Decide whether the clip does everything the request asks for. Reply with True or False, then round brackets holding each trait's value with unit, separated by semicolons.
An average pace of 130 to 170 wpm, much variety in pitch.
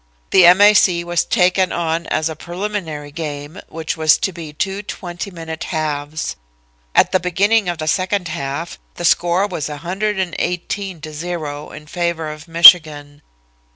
False (155 wpm; 3.0 semitones)